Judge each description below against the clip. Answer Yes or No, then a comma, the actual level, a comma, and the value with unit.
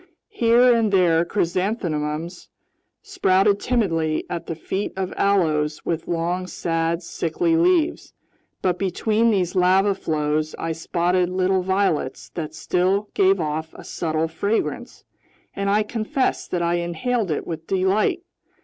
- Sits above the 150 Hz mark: Yes, medium, 185 Hz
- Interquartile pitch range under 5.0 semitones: Yes, average, 3.6 semitones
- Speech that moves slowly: Yes, slow, 130 wpm